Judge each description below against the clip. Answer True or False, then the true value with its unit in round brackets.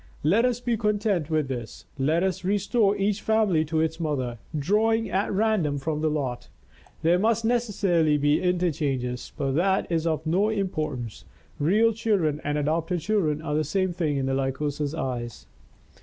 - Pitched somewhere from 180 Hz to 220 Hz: False (165 Hz)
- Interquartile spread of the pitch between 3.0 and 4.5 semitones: False (5.6 semitones)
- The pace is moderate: True (165 wpm)